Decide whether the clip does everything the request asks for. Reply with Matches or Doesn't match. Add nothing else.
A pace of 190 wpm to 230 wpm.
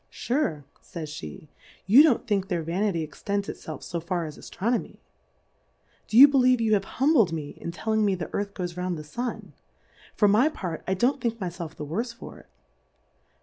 Matches